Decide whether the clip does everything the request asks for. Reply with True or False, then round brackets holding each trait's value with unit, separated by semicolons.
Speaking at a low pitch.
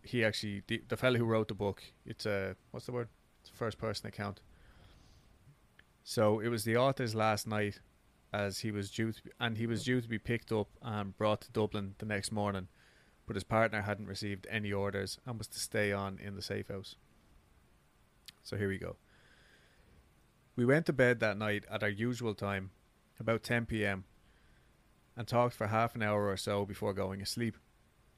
True (105 Hz)